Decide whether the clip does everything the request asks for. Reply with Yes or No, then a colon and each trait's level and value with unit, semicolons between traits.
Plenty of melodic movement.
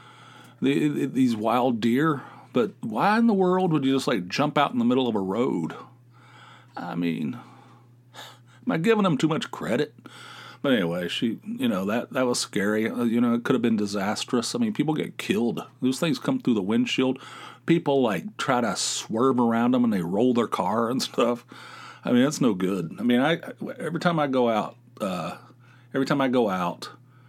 Yes: wide, 7.3 semitones